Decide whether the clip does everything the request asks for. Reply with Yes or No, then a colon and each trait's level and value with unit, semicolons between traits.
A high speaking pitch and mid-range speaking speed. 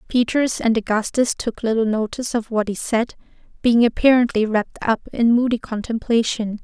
Yes: high, 230 Hz; average, 155 wpm